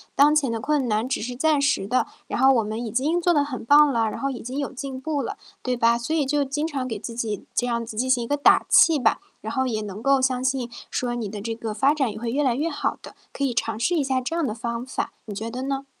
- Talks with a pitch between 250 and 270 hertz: Yes, very high, 255 Hz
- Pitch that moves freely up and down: No, average, 3.4 semitones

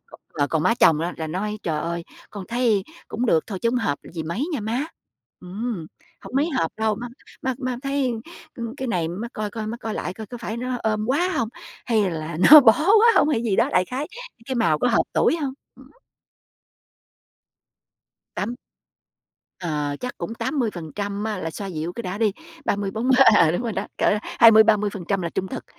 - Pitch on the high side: Yes, high, 215 Hz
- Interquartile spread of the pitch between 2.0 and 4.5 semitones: No, average, 5.2 semitones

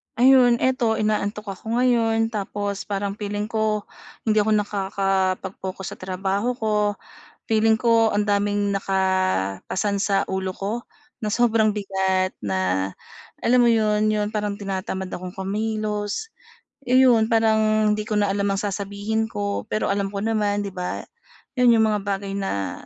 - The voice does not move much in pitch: Yes, narrow, 2.1 semitones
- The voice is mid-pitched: No, high, 205 Hz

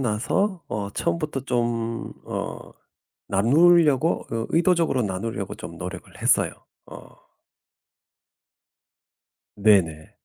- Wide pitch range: Yes, wide, 8.1 semitones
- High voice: No, low, 120 Hz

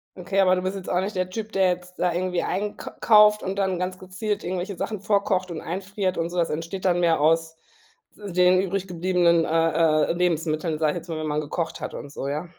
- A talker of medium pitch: Yes, medium, 180 Hz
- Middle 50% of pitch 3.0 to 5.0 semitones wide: No, narrow, 2.6 semitones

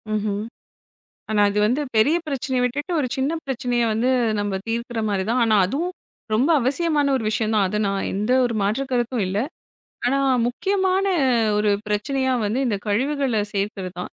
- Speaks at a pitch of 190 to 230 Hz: No, high, 240 Hz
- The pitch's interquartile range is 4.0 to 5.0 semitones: Yes, average, 4.6 semitones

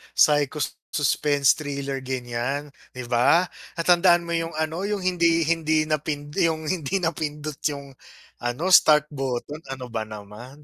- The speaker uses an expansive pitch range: No, average, 3.7 semitones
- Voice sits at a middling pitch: Yes, medium, 150 Hz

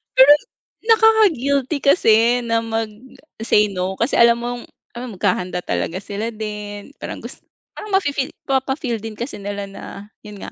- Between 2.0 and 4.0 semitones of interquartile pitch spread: No, average, 4.4 semitones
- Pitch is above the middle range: Yes, high, 230 Hz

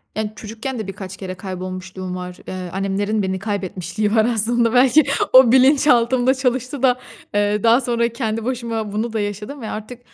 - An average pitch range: Yes, average, 3.9 semitones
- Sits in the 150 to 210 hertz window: No, high, 220 Hz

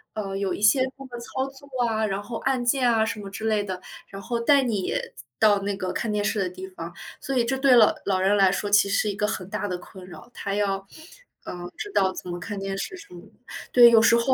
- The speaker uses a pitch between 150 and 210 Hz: Yes, high, 205 Hz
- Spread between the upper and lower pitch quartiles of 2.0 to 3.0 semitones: No, average, 3.4 semitones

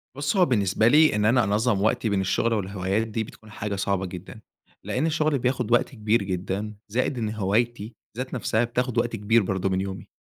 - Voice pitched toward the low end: Yes, low, 110 Hz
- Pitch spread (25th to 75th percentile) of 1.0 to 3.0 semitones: No, average, 3.5 semitones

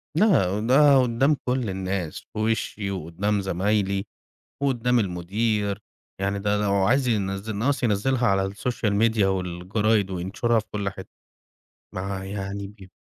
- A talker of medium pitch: No, low, 100 Hz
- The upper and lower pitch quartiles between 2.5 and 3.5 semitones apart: Yes, average, 3.0 semitones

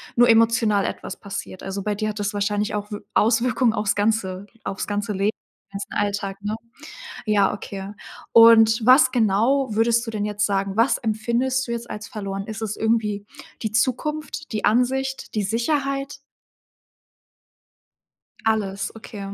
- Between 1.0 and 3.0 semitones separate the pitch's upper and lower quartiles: Yes, narrow, 2.5 semitones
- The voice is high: Yes, high, 215 Hz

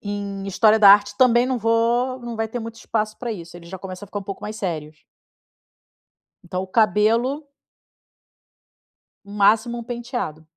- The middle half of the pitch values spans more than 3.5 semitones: No, average, 3.2 semitones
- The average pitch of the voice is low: No, high, 215 Hz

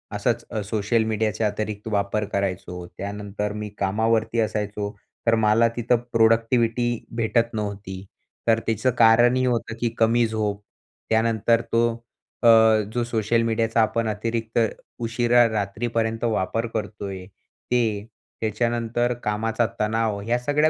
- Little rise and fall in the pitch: Yes, narrow, 1.9 semitones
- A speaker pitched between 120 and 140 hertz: No, low, 110 Hz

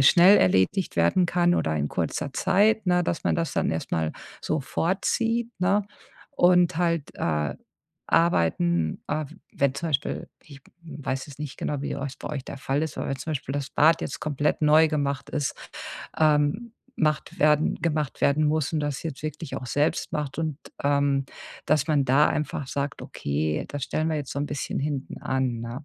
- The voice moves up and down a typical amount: Yes, average, 3.2 semitones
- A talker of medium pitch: Yes, medium, 145 Hz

